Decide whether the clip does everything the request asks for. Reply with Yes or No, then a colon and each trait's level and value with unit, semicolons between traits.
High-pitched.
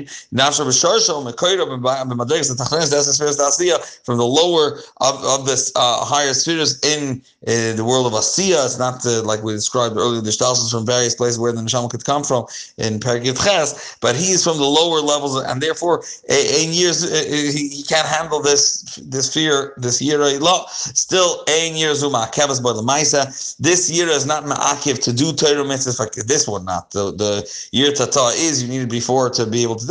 No: medium, 140 Hz